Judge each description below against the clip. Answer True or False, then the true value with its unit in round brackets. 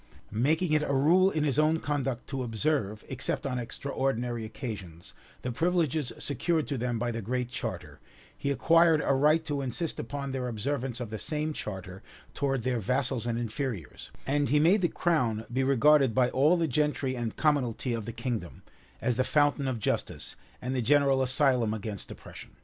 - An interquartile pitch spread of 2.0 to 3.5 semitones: False (3.9 semitones)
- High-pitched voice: False (130 Hz)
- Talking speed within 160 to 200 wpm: True (180 wpm)